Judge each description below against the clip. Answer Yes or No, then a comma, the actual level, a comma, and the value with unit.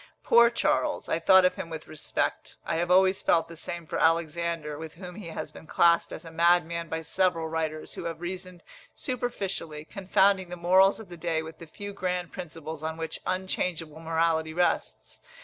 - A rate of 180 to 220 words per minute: Yes, average, 185 wpm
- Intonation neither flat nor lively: No, narrow, 2.2 semitones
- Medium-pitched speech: Yes, medium, 170 Hz